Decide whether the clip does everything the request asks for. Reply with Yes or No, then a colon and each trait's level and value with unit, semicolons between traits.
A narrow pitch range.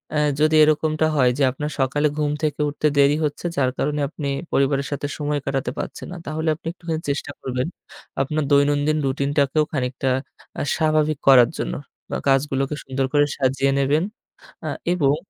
Yes: narrow, 2.0 semitones